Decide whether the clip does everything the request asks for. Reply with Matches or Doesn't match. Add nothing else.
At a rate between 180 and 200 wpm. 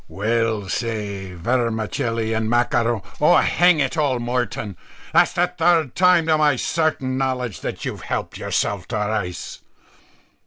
Doesn't match